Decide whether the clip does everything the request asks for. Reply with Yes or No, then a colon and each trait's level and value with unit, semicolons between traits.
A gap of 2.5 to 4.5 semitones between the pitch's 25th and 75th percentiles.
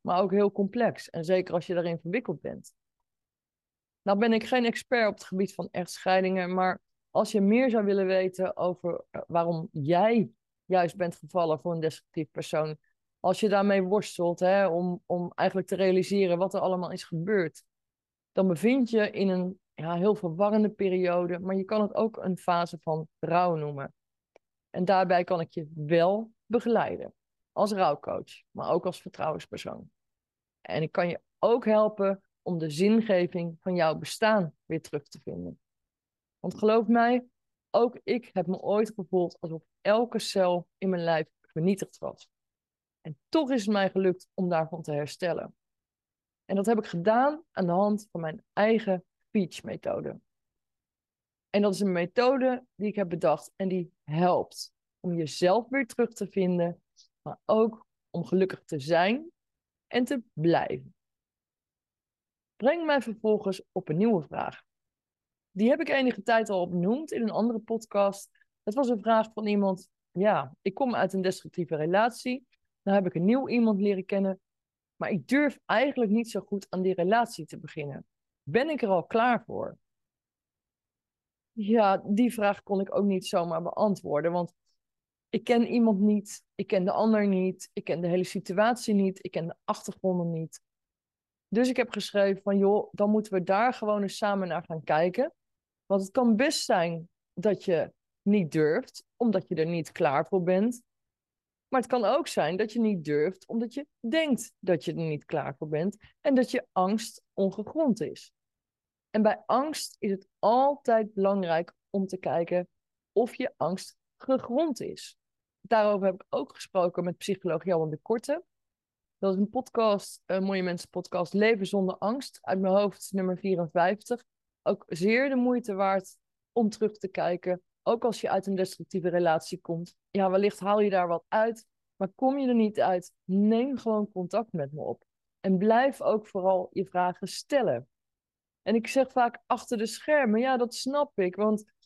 Yes: average, 3.9 semitones